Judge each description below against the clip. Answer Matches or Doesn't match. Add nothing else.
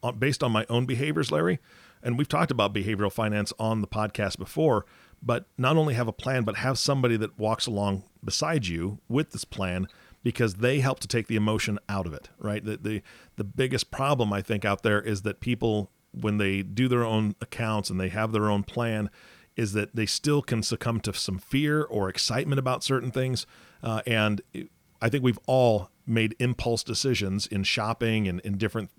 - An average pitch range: Matches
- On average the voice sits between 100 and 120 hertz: Matches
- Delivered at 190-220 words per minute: Matches